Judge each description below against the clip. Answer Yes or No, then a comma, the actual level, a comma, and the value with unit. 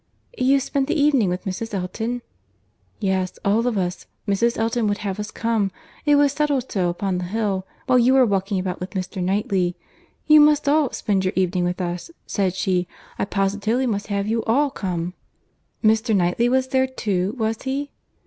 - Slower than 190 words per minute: Yes, average, 180 wpm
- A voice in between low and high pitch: No, high, 210 Hz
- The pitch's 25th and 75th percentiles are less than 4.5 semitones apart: No, average, 4.9 semitones